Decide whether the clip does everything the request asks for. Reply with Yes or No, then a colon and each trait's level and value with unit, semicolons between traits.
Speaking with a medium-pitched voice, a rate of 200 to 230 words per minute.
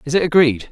No: medium, 145 Hz; fast, 250 wpm